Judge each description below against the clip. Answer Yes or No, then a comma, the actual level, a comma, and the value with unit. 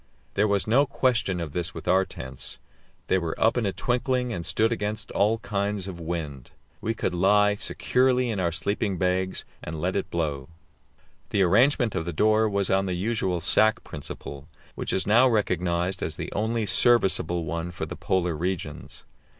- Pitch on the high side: No, very low, 95 Hz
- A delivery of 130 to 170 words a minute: No, average, 180 wpm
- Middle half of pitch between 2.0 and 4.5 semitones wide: Yes, average, 4.2 semitones